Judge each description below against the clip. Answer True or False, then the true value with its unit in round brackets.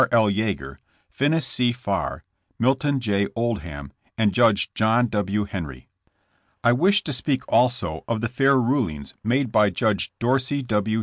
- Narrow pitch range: False (4.1 semitones)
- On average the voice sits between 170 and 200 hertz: False (115 Hz)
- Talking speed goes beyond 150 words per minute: False (145 wpm)